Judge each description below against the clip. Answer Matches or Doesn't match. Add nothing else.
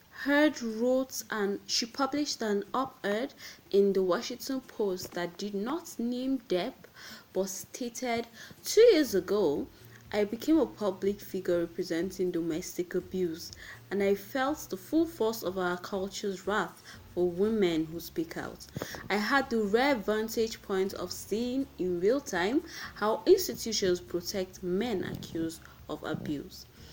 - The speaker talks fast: Doesn't match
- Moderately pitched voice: Doesn't match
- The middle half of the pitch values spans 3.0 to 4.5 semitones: Doesn't match